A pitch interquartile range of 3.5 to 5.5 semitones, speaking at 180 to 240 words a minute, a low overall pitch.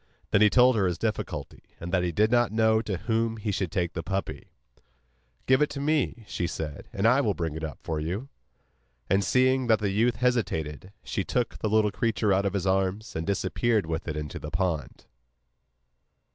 Yes: average, 4.6 semitones; average, 200 wpm; low, 100 Hz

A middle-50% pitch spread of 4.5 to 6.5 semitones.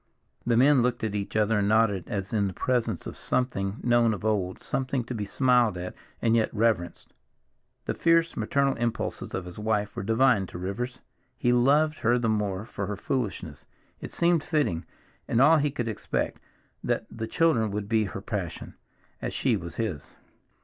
No: average, 3.8 semitones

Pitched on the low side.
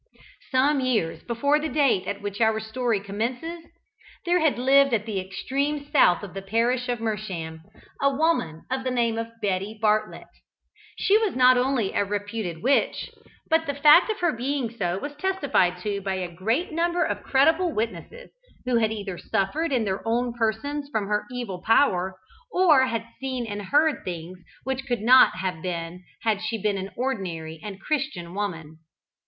No: high, 230 Hz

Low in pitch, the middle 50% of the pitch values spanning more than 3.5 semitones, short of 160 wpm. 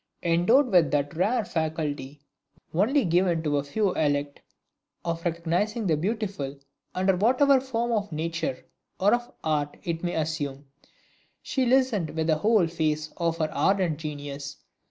No: medium, 165 Hz; average, 5.3 semitones; average, 145 wpm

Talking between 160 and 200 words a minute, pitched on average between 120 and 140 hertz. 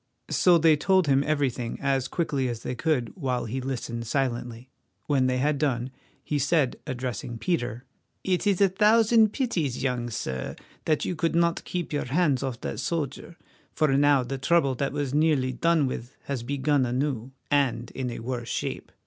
Yes: average, 175 wpm; low, 135 Hz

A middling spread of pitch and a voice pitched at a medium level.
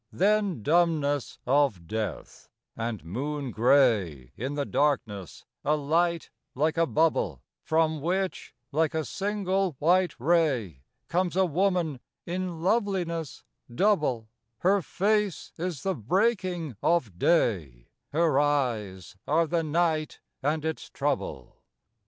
No: wide, 5.9 semitones; medium, 155 Hz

